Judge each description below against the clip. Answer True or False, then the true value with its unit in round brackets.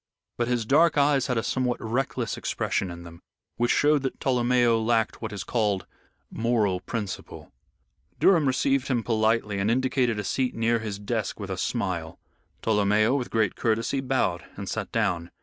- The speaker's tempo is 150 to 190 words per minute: True (165 wpm)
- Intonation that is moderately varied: True (3.6 semitones)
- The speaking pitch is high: False (115 Hz)